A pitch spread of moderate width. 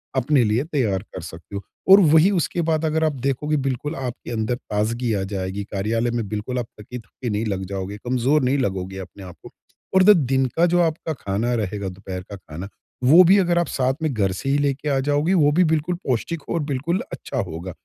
No: wide, 7.1 semitones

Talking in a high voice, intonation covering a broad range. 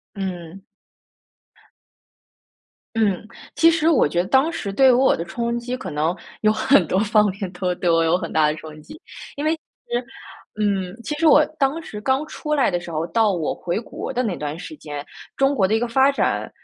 Yes: high, 215 Hz; wide, 7.3 semitones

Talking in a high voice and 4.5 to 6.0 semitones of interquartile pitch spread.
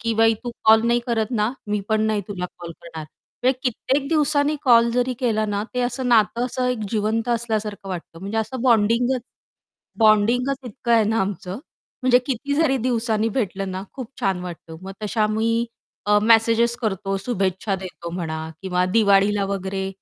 No: high, 220 Hz; average, 3.5 semitones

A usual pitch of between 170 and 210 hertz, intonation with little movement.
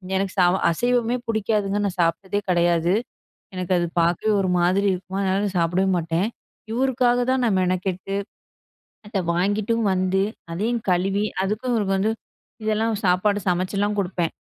No: high, 195 Hz; average, 3.0 semitones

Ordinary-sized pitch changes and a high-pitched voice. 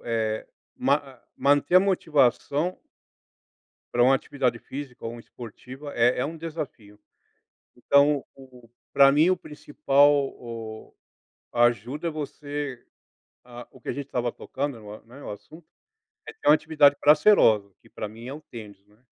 No: average, 3.9 semitones; low, 135 Hz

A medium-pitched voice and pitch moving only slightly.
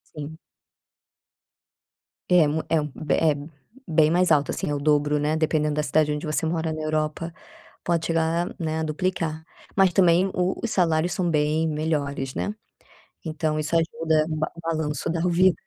Yes: medium, 160 Hz; narrow, 1.6 semitones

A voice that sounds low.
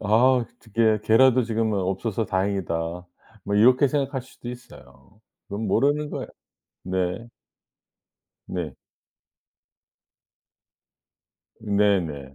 Yes: low, 110 Hz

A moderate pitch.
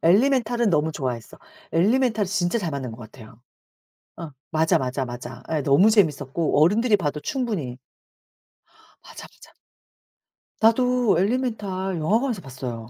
Yes: medium, 175 Hz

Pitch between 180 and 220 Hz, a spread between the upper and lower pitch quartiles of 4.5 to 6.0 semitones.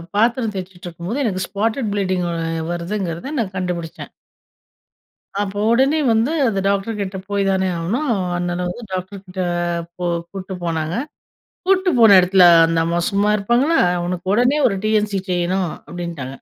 No: high, 195 Hz; average, 3.7 semitones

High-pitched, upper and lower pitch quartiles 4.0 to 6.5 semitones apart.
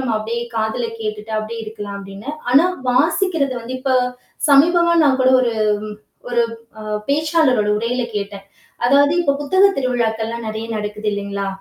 Yes: high, 235 Hz; average, 4.6 semitones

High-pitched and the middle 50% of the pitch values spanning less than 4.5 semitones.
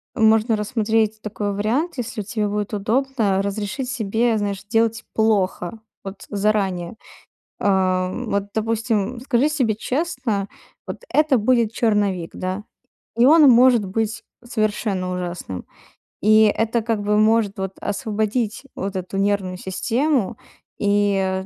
Yes: high, 215 Hz; average, 2.7 semitones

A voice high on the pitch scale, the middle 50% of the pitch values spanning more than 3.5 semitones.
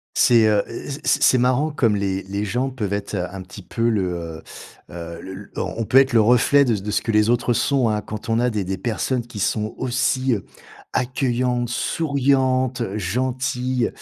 No: low, 115 Hz; average, 3.9 semitones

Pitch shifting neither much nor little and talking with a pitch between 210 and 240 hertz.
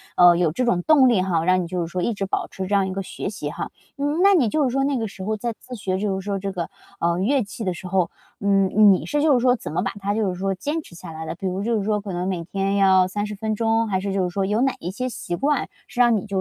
No: average, 4.1 semitones; high, 200 Hz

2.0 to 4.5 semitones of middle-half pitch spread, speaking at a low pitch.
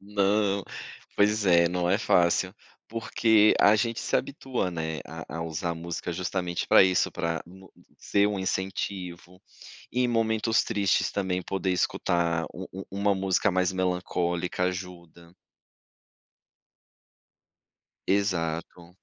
Yes: average, 2.7 semitones; very low, 95 Hz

